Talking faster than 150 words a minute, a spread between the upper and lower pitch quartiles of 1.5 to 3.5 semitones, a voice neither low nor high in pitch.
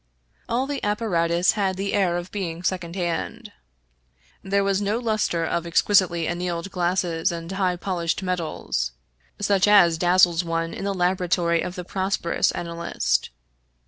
No: average, 145 wpm; narrow, 2.6 semitones; medium, 180 Hz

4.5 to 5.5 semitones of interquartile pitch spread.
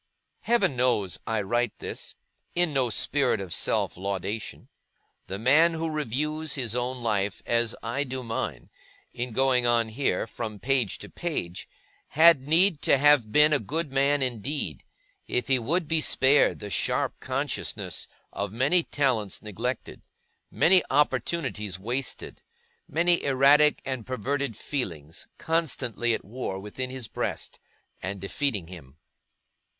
Yes: average, 5.1 semitones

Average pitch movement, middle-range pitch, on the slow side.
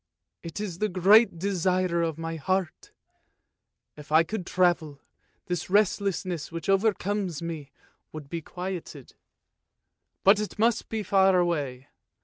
Yes: average, 3.1 semitones; medium, 180 Hz; slow, 130 wpm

